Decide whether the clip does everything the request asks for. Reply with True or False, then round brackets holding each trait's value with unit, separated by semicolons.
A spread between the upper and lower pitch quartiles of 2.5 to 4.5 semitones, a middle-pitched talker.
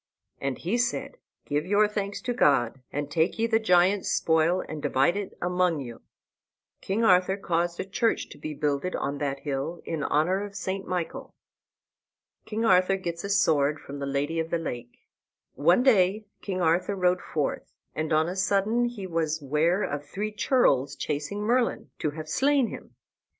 False (4.9 semitones; 175 Hz)